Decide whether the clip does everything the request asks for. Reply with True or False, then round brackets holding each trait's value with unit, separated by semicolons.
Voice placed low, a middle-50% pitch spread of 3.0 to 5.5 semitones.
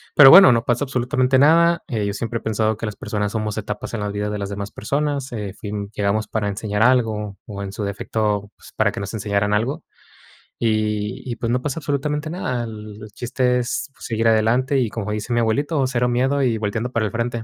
True (115 Hz; 3.5 semitones)